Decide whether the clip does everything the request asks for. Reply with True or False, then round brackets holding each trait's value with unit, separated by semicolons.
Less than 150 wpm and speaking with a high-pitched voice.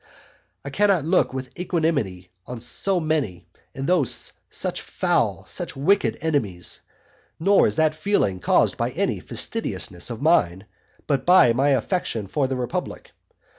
False (140 wpm; 140 Hz)